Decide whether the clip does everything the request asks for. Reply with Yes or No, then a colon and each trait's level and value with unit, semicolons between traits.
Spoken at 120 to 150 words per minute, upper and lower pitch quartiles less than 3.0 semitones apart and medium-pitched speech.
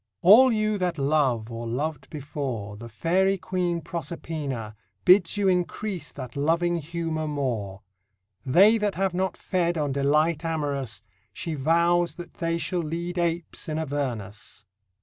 No: average, 140 wpm; average, 4.0 semitones; medium, 160 Hz